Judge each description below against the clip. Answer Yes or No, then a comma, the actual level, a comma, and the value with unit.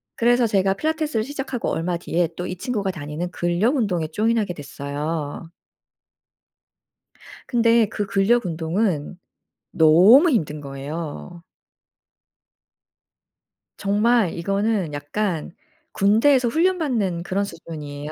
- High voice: Yes, high, 195 Hz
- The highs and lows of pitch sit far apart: Yes, wide, 6.0 semitones